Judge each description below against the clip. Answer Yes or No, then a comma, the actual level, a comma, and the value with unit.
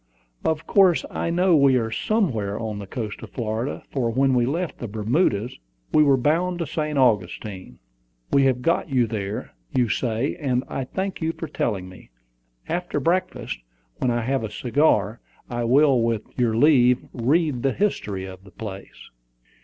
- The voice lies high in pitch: No, low, 125 Hz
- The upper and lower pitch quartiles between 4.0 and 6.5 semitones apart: Yes, wide, 5.6 semitones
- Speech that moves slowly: No, average, 170 wpm